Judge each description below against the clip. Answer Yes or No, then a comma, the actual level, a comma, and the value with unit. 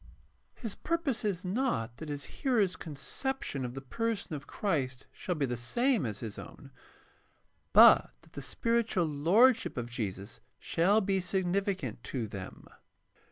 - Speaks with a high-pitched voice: No, medium, 175 Hz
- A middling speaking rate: Yes, average, 150 wpm